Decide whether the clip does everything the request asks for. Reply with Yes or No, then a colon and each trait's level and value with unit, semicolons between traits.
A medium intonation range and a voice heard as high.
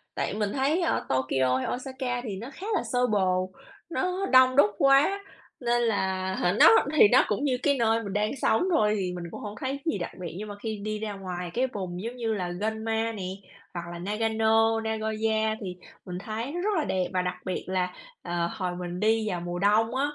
Yes: average, 4.6 semitones; high, 215 Hz